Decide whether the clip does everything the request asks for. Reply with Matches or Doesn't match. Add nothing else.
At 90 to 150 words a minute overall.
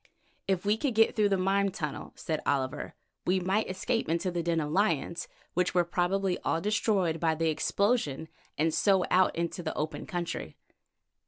Doesn't match